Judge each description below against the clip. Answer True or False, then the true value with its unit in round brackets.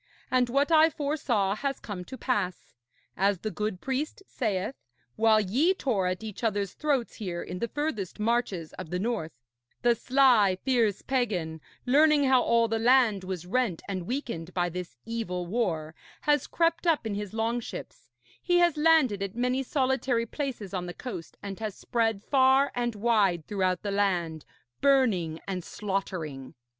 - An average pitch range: False (5.8 semitones)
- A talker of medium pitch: False (220 Hz)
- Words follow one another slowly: False (165 wpm)